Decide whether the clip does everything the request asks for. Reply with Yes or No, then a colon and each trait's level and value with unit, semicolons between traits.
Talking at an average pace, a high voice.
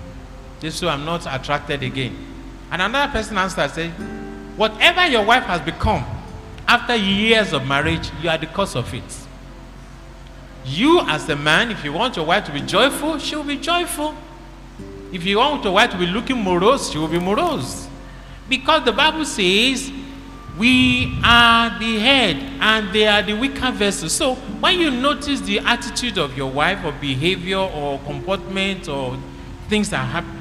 Yes: average, 170 wpm; high, 200 Hz